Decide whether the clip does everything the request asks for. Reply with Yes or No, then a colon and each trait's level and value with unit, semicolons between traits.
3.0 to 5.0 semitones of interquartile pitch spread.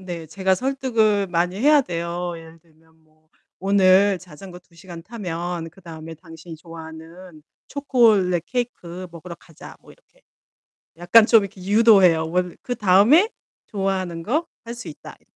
Yes: average, 3.9 semitones